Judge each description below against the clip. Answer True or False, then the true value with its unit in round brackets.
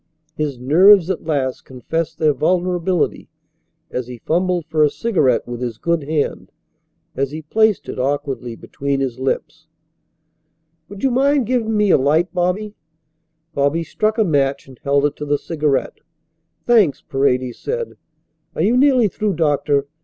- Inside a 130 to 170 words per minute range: True (155 wpm)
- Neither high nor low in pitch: True (155 Hz)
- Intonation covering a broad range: True (6.0 semitones)